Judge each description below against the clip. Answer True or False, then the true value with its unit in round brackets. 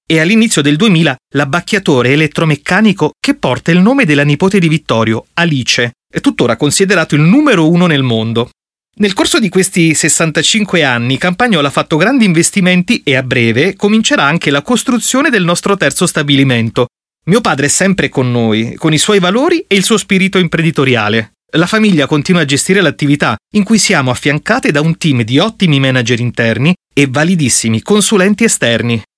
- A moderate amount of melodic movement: False (6.3 semitones)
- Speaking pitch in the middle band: True (160 Hz)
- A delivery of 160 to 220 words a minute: True (165 wpm)